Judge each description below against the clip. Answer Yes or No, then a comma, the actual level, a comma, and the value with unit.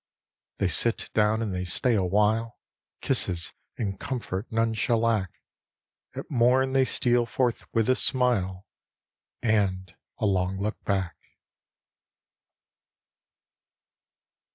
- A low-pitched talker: Yes, low, 110 Hz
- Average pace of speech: No, slow, 105 wpm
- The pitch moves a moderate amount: Yes, average, 3.8 semitones